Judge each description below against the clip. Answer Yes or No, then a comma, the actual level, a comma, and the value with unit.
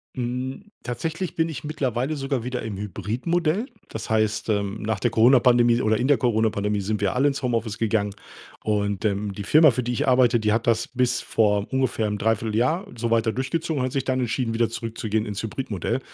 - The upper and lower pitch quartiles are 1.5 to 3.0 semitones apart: No, average, 3.4 semitones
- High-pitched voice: No, low, 115 Hz